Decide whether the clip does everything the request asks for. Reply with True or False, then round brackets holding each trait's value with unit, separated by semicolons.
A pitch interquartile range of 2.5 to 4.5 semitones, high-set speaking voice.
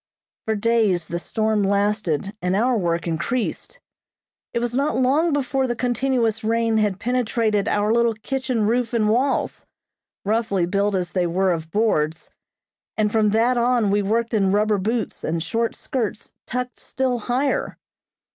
True (3.3 semitones; 220 Hz)